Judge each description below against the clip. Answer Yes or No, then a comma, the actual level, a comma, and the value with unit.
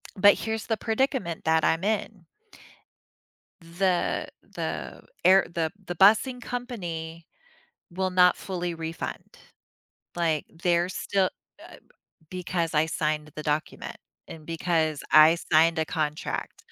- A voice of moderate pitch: Yes, medium, 170 Hz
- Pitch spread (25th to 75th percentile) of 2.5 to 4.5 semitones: Yes, average, 3.2 semitones